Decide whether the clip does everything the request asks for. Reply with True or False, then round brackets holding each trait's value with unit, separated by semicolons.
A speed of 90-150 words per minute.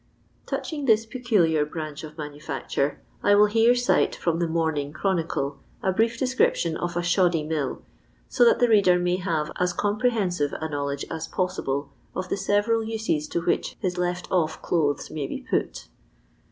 False (165 wpm)